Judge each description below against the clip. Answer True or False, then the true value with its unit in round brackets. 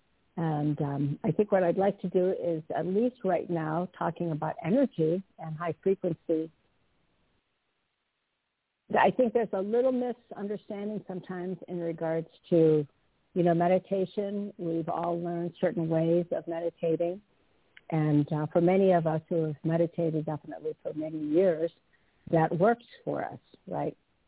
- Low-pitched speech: False (170 Hz)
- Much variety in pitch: False (3.0 semitones)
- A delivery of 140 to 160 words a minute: True (145 wpm)